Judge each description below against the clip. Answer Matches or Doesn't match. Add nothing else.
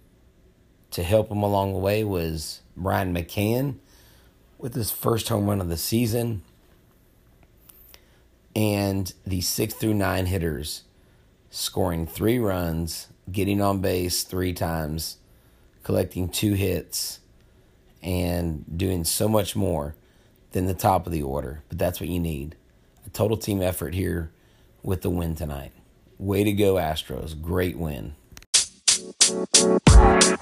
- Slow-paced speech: Matches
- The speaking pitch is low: Matches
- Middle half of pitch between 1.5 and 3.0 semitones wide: Doesn't match